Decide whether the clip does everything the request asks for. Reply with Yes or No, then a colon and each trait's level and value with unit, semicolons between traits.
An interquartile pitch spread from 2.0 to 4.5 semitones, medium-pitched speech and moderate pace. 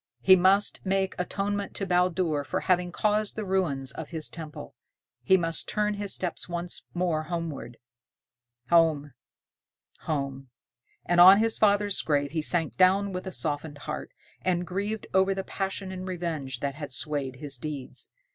Yes: average, 4.2 semitones; medium, 175 Hz; average, 155 wpm